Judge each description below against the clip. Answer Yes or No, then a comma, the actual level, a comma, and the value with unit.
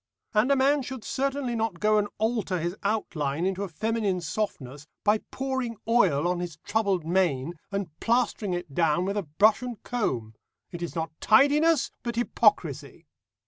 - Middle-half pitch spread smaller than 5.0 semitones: No, wide, 5.5 semitones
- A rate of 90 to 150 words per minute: No, average, 165 wpm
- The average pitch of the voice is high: Yes, high, 205 Hz